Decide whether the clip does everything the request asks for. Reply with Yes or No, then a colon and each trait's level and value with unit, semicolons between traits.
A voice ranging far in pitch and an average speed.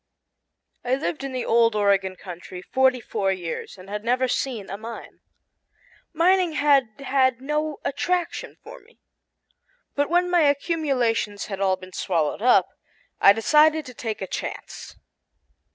Yes: wide, 6.7 semitones; average, 150 wpm